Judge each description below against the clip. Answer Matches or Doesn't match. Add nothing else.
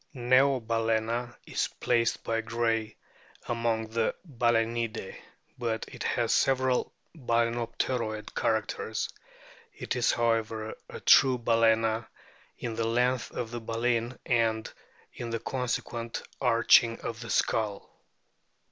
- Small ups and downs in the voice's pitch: Matches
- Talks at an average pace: Doesn't match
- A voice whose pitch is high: Doesn't match